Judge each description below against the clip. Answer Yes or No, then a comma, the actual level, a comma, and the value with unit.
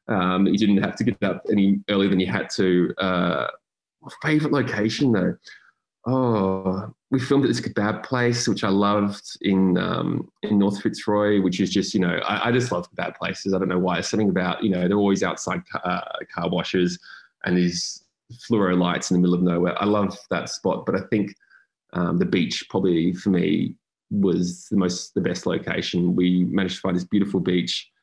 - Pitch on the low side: Yes, low, 100 Hz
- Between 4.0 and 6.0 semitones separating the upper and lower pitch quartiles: No, average, 2.8 semitones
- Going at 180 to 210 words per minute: Yes, average, 200 wpm